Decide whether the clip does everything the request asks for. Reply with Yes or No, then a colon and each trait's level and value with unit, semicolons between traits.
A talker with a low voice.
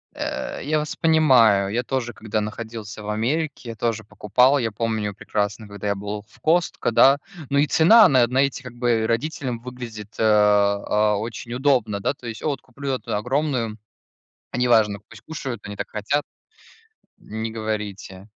Yes: low, 115 Hz